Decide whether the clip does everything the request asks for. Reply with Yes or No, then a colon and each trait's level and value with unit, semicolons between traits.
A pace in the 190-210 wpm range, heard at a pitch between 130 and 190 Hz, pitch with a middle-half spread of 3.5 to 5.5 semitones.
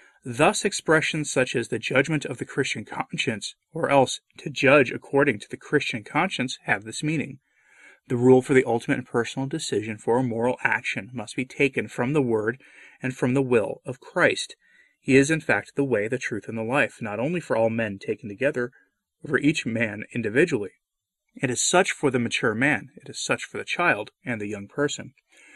Yes: average, 200 wpm; low, 135 Hz; average, 4.3 semitones